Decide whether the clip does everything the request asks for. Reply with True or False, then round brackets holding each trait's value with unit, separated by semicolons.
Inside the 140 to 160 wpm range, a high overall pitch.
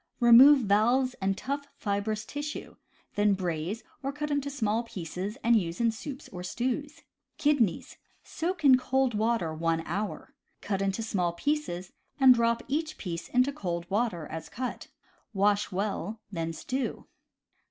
True (150 wpm; 220 Hz)